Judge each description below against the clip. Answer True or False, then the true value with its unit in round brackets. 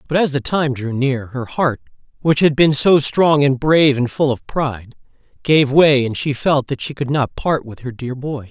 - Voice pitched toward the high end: False (135 Hz)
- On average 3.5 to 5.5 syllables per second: True (4.7 syllables/s)